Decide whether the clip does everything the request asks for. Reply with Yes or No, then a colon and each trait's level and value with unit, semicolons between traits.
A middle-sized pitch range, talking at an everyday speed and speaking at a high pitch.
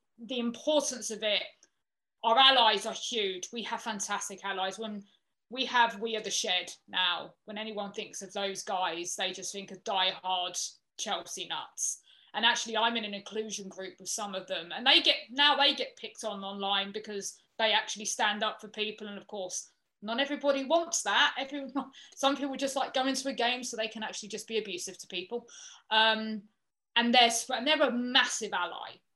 Yes: average, 4.4 semitones; average, 190 wpm; high, 220 Hz